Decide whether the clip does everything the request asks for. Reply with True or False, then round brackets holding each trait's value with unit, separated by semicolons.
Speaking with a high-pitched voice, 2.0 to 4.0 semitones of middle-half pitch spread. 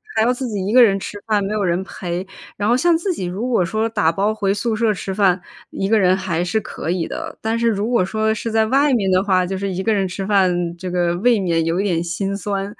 True (200 Hz; 3.1 semitones)